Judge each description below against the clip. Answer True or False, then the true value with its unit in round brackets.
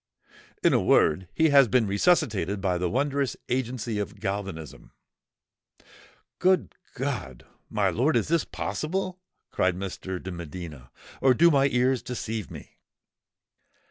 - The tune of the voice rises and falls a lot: True (6.7 semitones)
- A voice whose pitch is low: True (115 Hz)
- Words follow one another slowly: True (125 wpm)